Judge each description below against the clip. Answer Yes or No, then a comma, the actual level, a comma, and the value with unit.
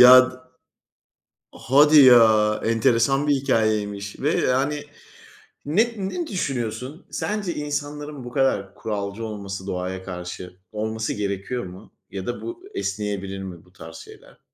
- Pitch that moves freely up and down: Yes, wide, 6.2 semitones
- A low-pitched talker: Yes, low, 115 Hz